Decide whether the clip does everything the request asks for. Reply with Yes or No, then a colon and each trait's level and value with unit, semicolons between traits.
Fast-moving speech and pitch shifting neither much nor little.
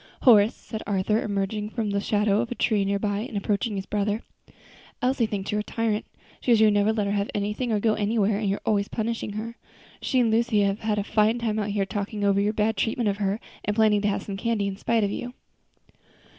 No: fast, 235 wpm; narrow, 1.7 semitones